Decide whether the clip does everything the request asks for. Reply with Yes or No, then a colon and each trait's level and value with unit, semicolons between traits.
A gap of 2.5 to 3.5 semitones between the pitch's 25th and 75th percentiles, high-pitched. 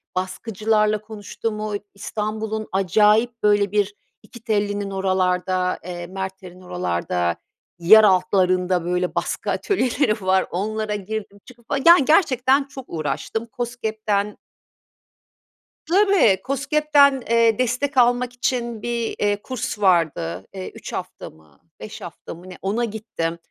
No: average, 4.2 semitones; high, 210 Hz